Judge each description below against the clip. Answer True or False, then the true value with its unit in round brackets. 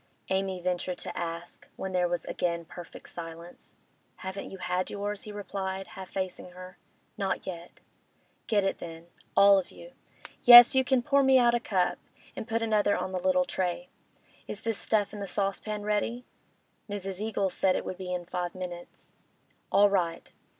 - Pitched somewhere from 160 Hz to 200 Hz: True (190 Hz)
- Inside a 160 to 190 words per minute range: True (170 wpm)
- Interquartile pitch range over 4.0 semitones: False (2.8 semitones)